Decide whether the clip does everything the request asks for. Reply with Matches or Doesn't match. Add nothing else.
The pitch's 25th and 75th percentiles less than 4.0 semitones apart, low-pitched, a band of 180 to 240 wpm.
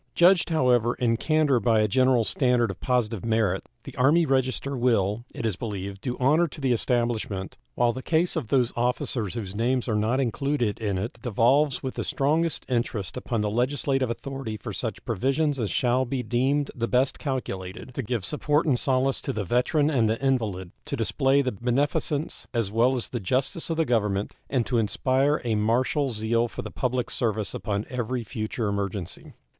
Matches